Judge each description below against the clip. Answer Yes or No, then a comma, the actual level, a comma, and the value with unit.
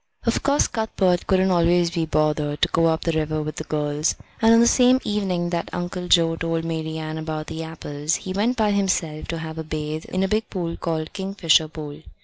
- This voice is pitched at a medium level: Yes, medium, 165 Hz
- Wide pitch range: No, average, 3.2 semitones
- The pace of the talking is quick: Yes, fast, 210 wpm